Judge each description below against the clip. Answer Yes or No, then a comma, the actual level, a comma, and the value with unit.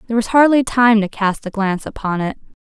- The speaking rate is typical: No, fast, 230 wpm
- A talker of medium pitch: No, high, 220 Hz